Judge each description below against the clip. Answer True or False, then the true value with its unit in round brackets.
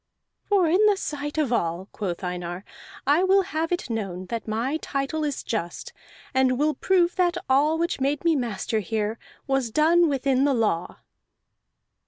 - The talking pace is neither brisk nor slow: True (165 wpm)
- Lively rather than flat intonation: True (6.5 semitones)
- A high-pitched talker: True (275 Hz)